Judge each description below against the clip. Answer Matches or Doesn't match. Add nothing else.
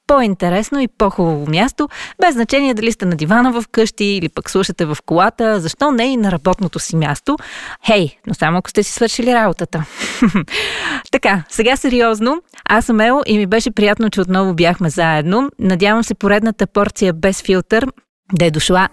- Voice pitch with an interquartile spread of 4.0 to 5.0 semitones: Matches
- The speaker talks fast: Matches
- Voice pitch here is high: Matches